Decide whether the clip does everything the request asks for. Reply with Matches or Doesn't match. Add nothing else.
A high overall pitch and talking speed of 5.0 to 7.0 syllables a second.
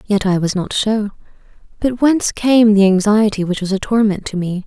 Matches